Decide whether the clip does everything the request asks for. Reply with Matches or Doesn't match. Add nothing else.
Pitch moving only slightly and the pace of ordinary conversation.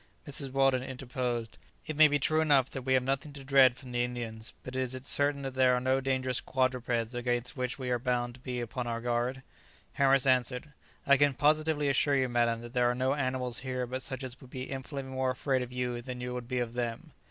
Doesn't match